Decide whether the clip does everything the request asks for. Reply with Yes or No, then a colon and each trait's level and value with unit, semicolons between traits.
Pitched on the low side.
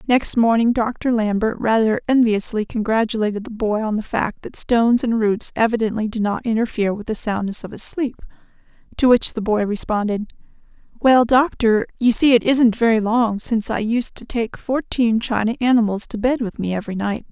No: high, 225 Hz